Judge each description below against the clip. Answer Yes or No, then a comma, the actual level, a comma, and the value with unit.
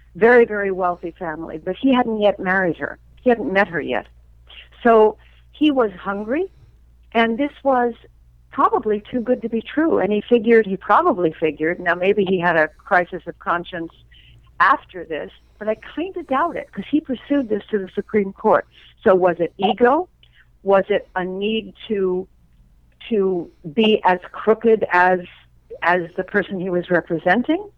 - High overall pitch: Yes, high, 195 Hz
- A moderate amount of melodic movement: Yes, average, 4.7 semitones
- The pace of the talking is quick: No, average, 170 wpm